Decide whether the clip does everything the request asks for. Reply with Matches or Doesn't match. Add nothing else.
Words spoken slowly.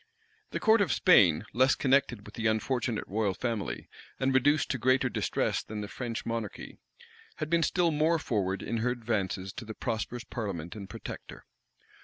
Doesn't match